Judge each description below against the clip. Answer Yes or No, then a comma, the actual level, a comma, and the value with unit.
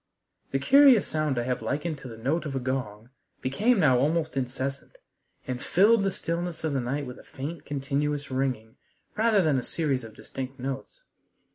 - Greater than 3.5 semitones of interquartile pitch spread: Yes, average, 4.4 semitones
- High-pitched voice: No, medium, 140 Hz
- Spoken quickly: No, average, 180 wpm